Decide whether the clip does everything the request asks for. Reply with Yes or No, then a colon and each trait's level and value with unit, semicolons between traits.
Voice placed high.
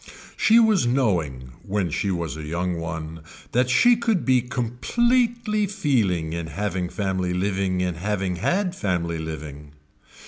No: very low, 95 Hz